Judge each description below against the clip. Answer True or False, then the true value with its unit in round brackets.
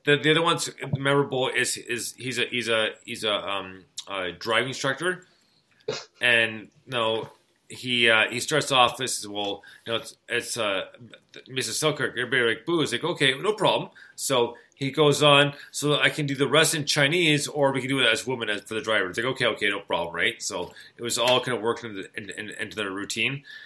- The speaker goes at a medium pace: False (220 wpm)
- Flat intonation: False (4.4 semitones)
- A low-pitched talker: True (130 Hz)